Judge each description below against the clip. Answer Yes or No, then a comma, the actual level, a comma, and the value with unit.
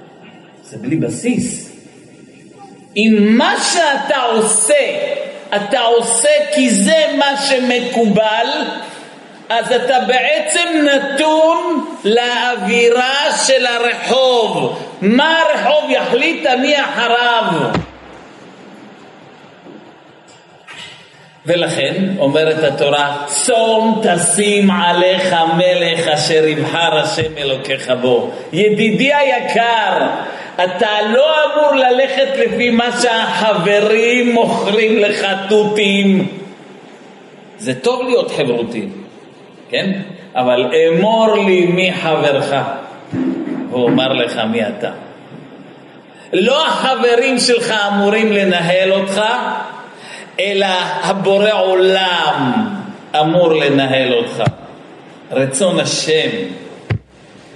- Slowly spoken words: Yes, slow, 80 wpm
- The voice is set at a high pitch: Yes, high, 220 Hz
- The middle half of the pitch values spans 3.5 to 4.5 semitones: No, average, 5.2 semitones